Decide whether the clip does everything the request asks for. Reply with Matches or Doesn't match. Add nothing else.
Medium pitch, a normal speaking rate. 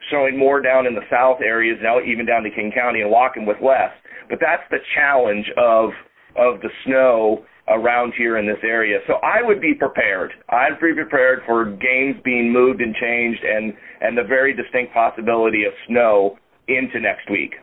Doesn't match